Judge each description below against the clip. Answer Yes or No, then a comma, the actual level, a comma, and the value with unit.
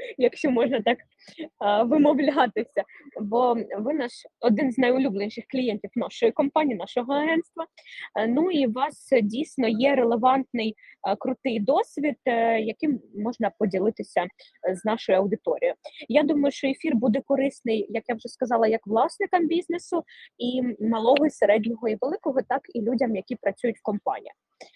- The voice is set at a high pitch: Yes, very high, 250 Hz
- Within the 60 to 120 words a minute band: No, average, 135 wpm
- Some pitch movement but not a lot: Yes, average, 4.3 semitones